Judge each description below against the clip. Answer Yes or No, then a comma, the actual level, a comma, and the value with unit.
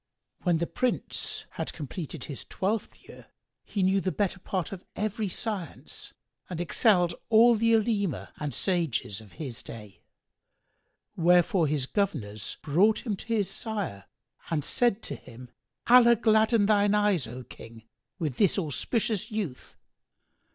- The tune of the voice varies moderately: No, wide, 6.2 semitones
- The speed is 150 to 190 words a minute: No, average, 140 wpm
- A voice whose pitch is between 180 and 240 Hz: Yes, high, 190 Hz